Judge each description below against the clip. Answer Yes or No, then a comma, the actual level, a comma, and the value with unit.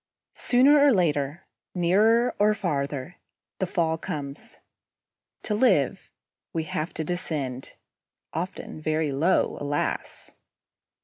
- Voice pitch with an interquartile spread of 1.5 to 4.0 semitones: No, wide, 5.6 semitones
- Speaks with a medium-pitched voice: Yes, medium, 165 Hz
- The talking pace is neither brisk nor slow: No, slow, 105 wpm